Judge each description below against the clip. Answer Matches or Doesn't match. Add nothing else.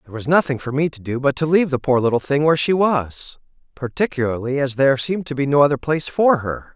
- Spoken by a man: Matches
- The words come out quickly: Matches